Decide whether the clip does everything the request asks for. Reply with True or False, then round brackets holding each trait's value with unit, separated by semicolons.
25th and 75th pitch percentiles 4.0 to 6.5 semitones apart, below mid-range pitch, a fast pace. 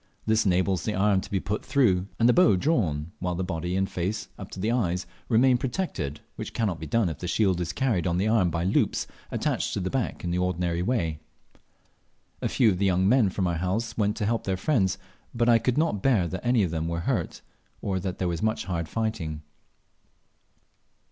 True (4.3 semitones; 95 Hz; 220 wpm)